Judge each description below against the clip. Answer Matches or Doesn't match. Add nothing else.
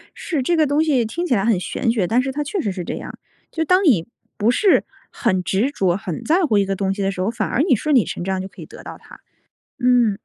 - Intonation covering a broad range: Matches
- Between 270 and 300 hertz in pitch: Doesn't match